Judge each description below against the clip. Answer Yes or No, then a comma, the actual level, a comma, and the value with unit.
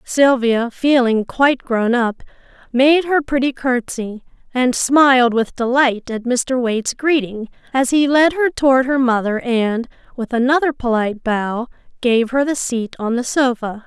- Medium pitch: No, very high, 250 Hz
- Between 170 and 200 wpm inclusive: No, average, 155 wpm